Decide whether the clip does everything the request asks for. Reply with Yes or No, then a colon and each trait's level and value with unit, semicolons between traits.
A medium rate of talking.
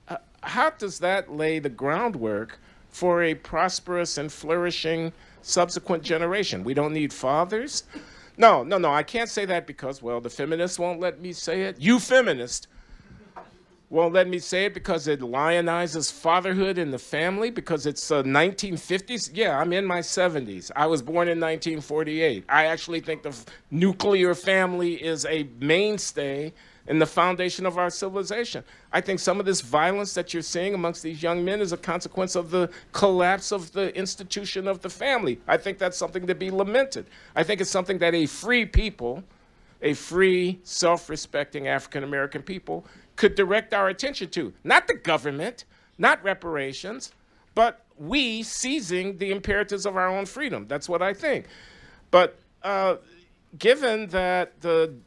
Yes: average, 165 wpm